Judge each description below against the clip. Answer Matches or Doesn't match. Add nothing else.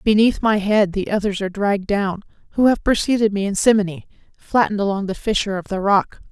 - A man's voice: Doesn't match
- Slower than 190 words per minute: Doesn't match